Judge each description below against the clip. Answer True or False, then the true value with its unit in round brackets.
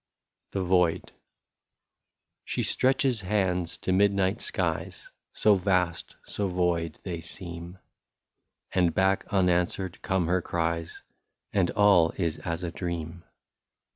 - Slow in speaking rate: True (120 wpm)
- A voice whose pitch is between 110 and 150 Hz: False (90 Hz)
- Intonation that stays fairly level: True (2.2 semitones)